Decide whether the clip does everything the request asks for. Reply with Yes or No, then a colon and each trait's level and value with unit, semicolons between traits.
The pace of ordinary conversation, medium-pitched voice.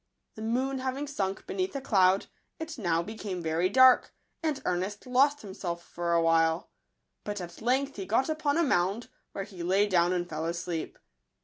No: average, 185 wpm; high, 200 Hz